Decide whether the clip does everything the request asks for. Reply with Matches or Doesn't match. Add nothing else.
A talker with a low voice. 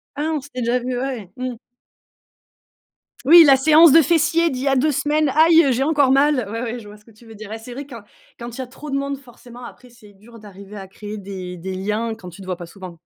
Doesn't match